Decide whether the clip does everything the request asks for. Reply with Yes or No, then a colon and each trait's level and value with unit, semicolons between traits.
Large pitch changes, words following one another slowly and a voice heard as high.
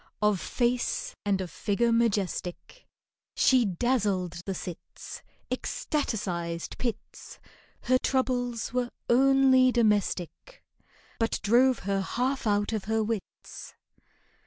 No: average, 4.3 semitones; slow, 105 wpm; high, 225 Hz